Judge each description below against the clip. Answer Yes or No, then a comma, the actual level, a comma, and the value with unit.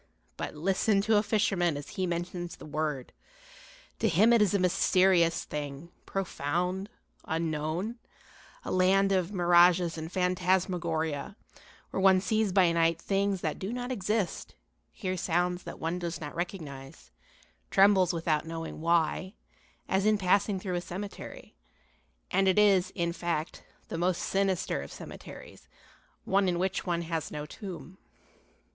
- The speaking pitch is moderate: Yes, medium, 180 Hz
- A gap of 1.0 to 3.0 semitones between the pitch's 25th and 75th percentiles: Yes, average, 2.7 semitones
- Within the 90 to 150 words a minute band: Yes, average, 145 wpm